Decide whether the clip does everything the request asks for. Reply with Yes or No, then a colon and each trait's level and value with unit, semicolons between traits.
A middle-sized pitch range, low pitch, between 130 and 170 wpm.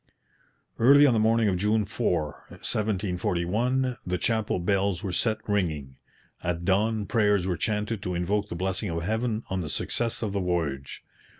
Yes: average, 3.8 semitones; low, 100 Hz; average, 165 wpm